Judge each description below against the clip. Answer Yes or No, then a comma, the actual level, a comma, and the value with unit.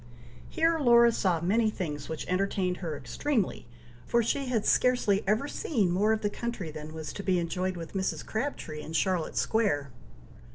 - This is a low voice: No, high, 195 Hz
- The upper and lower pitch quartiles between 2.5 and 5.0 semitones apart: No, wide, 5.6 semitones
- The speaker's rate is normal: Yes, average, 170 wpm